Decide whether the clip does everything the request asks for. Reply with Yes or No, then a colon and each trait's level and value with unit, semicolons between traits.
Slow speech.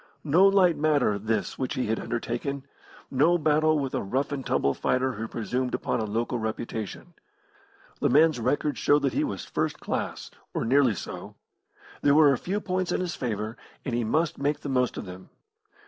No: average, 190 wpm